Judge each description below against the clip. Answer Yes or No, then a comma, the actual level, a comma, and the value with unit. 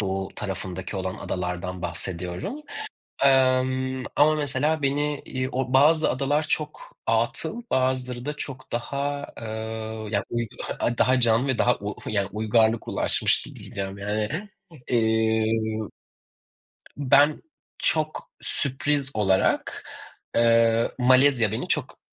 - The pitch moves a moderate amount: Yes, average, 4.7 semitones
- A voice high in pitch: No, low, 125 Hz